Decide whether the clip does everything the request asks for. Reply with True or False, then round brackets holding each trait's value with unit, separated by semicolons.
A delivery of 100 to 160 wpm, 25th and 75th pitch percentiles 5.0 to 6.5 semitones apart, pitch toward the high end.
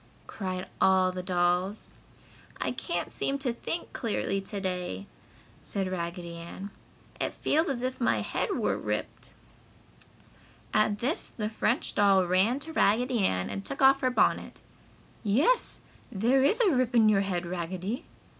True (150 wpm; 5.4 semitones; 200 Hz)